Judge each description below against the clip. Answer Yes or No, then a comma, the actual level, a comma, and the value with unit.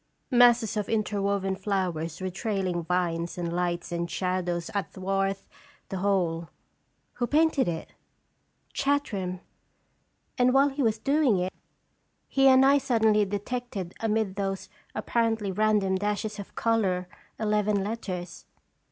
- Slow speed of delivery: Yes, slow, 125 wpm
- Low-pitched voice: No, high, 200 Hz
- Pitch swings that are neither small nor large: Yes, average, 3.6 semitones